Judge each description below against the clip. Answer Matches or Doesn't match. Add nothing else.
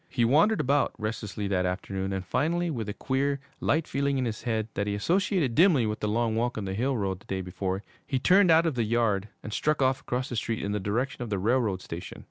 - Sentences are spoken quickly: Matches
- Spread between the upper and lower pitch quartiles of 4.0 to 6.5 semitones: Matches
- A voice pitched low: Matches